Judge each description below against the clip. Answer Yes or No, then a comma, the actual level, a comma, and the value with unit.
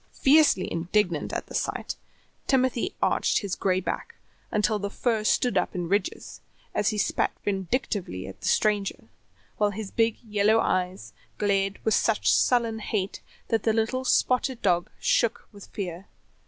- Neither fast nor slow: Yes, average, 155 wpm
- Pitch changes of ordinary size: Yes, average, 3.1 semitones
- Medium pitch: No, high, 210 Hz